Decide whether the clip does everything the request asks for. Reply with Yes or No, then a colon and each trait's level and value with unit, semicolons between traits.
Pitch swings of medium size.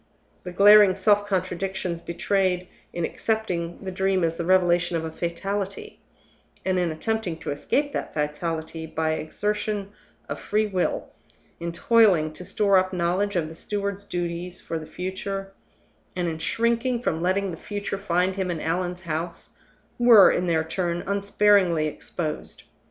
Yes: average, 3.0 semitones